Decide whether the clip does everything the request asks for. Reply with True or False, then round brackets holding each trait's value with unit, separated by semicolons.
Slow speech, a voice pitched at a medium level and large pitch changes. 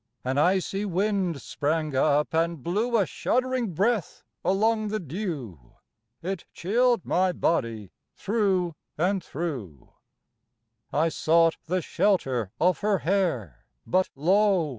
False (120 wpm; 175 Hz; 5.0 semitones)